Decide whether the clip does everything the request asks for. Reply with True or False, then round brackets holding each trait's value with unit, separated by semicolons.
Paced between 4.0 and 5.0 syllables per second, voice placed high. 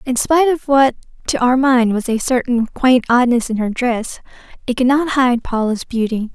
True (4.8 syllables/s; 250 Hz)